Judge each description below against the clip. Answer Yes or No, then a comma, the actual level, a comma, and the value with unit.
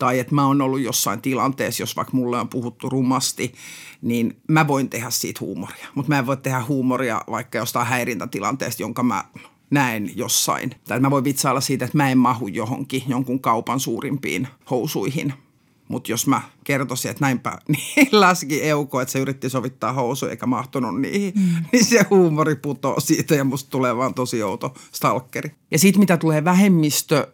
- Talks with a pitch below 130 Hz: No, low, 135 Hz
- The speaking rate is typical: No, fast, 180 wpm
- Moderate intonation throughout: Yes, average, 3.0 semitones